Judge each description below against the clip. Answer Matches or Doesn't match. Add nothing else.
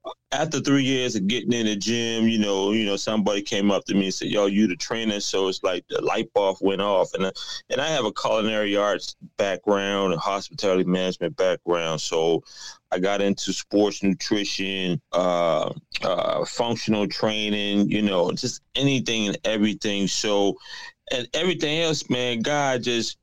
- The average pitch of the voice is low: Matches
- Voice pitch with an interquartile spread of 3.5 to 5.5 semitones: Doesn't match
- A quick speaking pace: Doesn't match